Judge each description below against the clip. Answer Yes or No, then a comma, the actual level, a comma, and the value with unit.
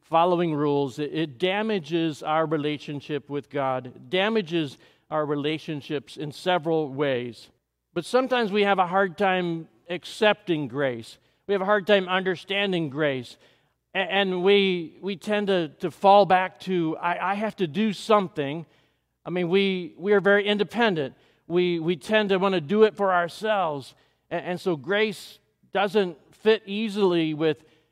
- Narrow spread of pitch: No, average, 4.4 semitones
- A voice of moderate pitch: Yes, medium, 180 Hz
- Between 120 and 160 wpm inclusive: Yes, average, 145 wpm